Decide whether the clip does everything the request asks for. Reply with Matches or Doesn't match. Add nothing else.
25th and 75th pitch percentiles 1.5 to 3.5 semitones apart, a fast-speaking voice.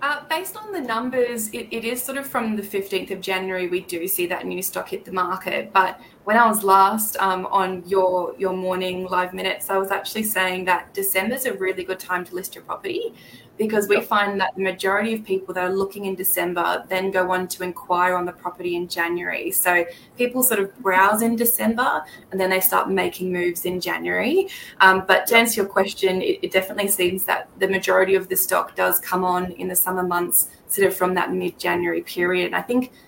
Matches